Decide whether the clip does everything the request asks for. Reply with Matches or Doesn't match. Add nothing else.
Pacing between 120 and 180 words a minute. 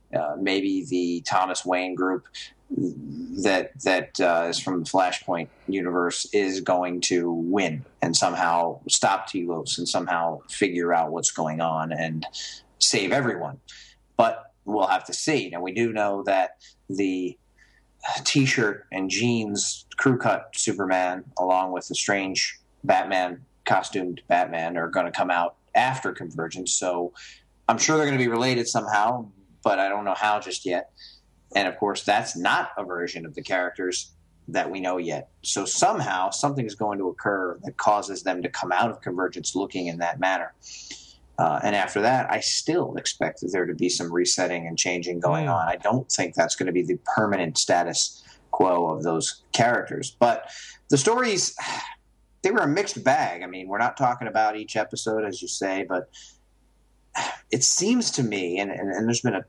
Matches